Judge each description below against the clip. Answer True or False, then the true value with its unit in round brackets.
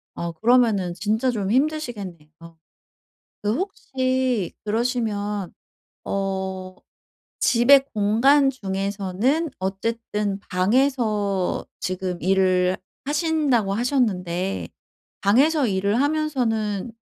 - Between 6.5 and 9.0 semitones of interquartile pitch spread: False (5.2 semitones)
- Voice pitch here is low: False (215 Hz)